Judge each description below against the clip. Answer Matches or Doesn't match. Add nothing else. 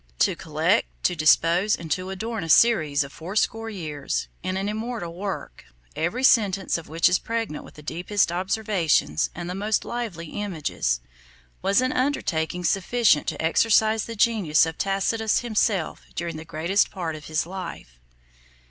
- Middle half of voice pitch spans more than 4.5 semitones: Matches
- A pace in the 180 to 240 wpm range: Doesn't match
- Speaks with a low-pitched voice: Doesn't match